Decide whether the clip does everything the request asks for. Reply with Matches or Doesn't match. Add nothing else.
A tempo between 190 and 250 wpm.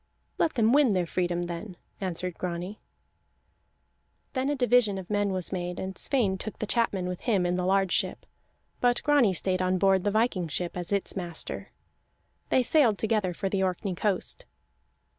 Doesn't match